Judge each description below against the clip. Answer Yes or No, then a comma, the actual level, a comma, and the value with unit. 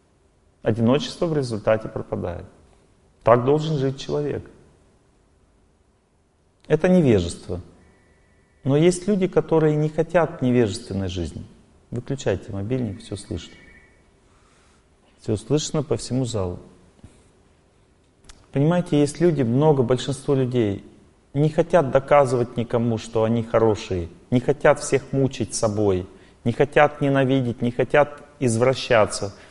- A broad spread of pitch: Yes, wide, 6.8 semitones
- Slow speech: Yes, slow, 105 wpm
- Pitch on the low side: Yes, low, 115 Hz